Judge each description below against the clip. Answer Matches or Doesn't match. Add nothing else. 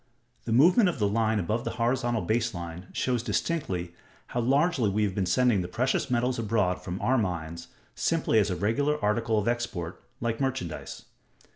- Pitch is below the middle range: Matches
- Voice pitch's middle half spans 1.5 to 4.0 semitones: Doesn't match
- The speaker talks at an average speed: Matches